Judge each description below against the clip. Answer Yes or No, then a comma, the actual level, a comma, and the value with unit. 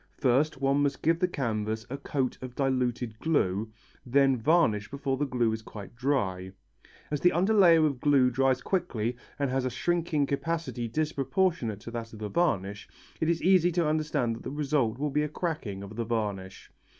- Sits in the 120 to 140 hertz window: Yes, low, 135 Hz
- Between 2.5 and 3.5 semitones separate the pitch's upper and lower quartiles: No, average, 5.2 semitones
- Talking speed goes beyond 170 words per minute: Yes, average, 185 wpm